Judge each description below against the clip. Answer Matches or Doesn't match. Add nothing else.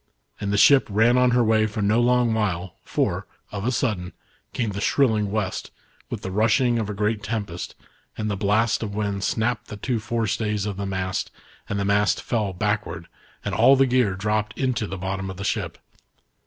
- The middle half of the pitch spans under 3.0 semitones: Matches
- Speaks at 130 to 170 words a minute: Doesn't match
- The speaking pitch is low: Matches